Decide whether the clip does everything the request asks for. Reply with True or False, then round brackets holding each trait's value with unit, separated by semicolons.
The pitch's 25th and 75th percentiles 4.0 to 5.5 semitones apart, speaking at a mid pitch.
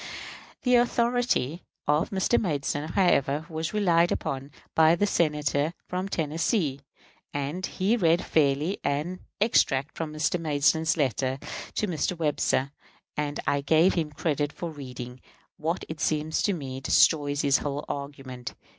False (3.4 semitones; 155 Hz)